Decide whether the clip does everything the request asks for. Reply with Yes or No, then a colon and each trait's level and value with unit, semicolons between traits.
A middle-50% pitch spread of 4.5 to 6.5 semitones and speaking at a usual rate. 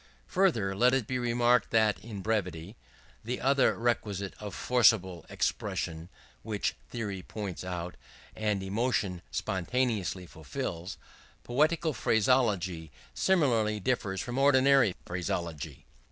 No: average, 5.1 semitones; slow, 110 wpm